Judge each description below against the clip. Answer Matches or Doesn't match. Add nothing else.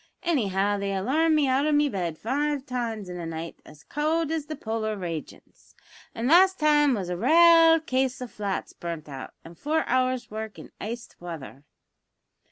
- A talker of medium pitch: Doesn't match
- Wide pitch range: Matches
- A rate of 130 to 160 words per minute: Doesn't match